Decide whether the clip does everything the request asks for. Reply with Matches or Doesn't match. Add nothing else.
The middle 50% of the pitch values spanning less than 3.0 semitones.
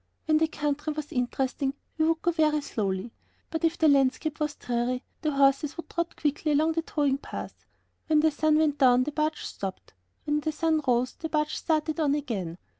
Matches